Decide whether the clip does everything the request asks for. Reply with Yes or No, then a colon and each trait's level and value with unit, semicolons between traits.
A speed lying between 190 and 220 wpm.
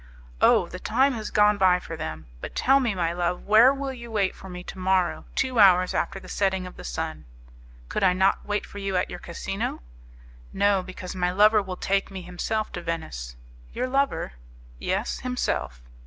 Yes: average, 195 wpm